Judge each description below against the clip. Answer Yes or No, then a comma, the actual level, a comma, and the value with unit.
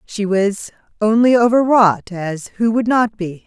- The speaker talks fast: No, average, 175 wpm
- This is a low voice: No, high, 210 Hz